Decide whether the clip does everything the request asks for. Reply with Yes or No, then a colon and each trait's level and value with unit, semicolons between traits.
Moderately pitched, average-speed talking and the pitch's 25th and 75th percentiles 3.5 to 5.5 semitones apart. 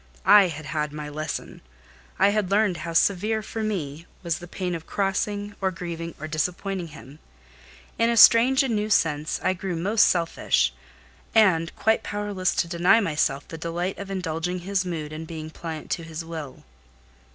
Yes: medium, 175 Hz; average, 175 wpm; average, 3.9 semitones